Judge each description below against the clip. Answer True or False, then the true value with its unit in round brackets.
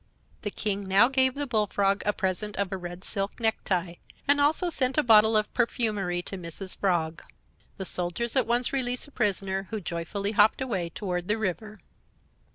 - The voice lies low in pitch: False (205 Hz)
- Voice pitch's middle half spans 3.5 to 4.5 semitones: True (4.1 semitones)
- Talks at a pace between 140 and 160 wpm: False (175 wpm)